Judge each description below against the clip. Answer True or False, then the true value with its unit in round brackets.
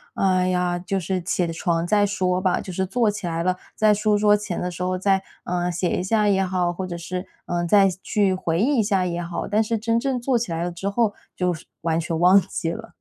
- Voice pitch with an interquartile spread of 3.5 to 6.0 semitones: False (2.8 semitones)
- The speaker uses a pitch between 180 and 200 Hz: True (185 Hz)